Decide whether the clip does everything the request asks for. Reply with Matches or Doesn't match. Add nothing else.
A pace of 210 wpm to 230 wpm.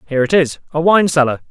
Doesn't match